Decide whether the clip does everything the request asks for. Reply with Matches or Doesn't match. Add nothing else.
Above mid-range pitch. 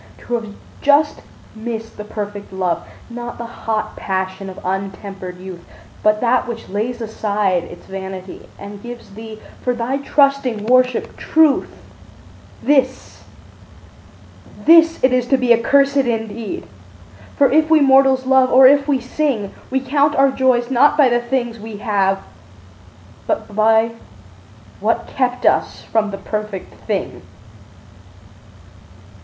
Matches